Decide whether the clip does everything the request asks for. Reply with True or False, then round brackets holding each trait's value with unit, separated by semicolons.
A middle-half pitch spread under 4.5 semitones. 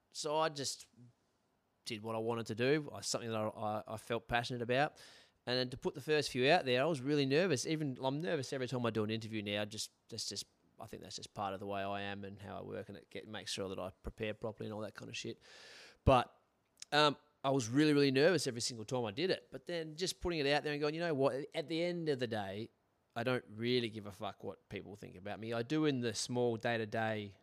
False (4.9 semitones)